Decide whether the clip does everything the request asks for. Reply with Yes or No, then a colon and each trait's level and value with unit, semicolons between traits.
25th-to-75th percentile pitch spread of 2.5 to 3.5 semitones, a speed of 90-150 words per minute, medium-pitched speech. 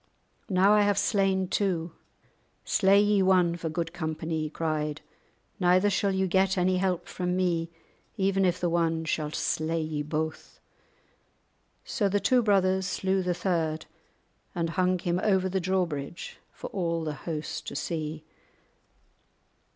Yes: average, 2.8 semitones; average, 145 wpm; medium, 180 Hz